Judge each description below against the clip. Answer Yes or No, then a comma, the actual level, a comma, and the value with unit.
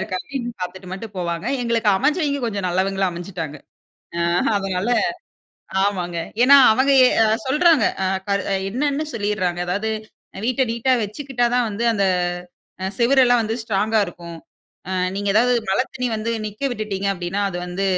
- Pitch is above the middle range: Yes, high, 210 Hz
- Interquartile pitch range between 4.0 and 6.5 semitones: Yes, average, 4.6 semitones